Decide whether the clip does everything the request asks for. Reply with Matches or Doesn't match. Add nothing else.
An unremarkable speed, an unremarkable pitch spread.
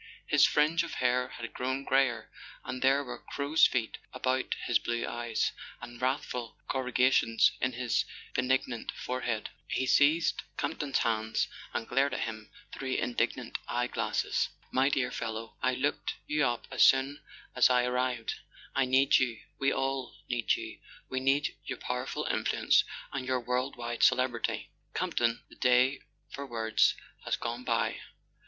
Doesn't match